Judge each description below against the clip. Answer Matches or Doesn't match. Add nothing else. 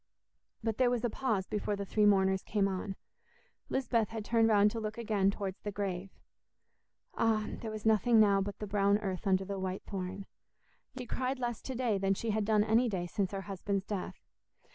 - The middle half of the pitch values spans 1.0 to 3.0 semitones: Matches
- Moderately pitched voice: Doesn't match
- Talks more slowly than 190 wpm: Doesn't match